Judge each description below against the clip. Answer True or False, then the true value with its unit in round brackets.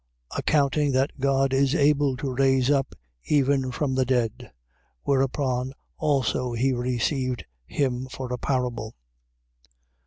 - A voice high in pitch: False (130 Hz)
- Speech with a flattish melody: True (1.6 semitones)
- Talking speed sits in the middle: False (120 wpm)